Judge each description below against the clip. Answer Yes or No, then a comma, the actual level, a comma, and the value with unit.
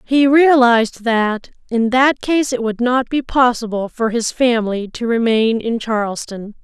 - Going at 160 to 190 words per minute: Yes, average, 165 wpm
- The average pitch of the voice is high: Yes, high, 235 Hz